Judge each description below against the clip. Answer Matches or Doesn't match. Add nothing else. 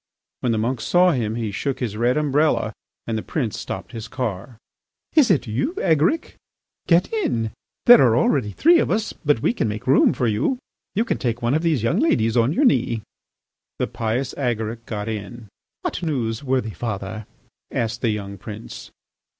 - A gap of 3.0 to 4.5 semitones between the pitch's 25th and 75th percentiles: Doesn't match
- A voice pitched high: Doesn't match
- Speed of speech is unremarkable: Matches